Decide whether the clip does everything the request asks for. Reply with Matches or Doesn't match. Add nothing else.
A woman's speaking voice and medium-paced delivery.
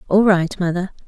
Matches